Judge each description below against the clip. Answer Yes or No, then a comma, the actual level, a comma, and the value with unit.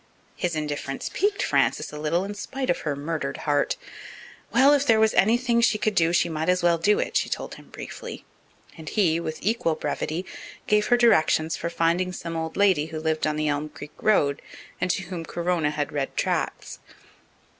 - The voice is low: No, medium, 170 Hz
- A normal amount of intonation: Yes, average, 5.0 semitones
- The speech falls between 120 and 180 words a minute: No, average, 195 wpm